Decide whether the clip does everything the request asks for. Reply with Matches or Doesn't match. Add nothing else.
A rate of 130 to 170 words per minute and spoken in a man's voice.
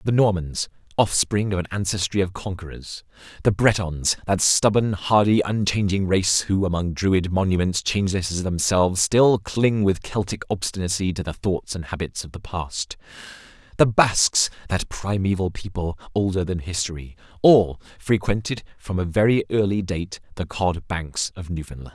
Matches